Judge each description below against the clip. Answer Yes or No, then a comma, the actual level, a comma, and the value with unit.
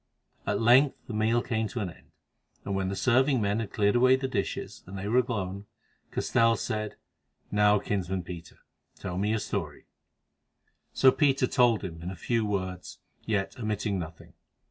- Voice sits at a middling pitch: No, low, 105 Hz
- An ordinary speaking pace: Yes, average, 165 wpm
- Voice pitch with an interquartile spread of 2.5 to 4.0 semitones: Yes, average, 3.7 semitones